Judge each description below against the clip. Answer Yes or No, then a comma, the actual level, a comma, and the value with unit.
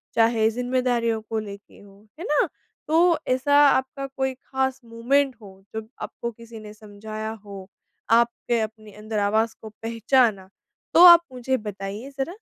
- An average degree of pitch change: Yes, average, 3.4 semitones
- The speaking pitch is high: Yes, high, 225 Hz